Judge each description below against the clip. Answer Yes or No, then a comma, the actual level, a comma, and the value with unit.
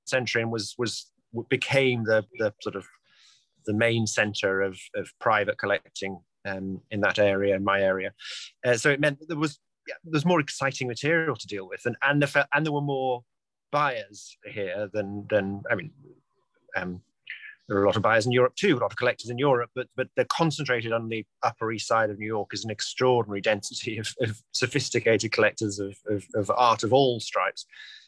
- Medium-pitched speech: No, low, 115 Hz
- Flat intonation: No, average, 4.9 semitones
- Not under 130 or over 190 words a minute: No, fast, 205 wpm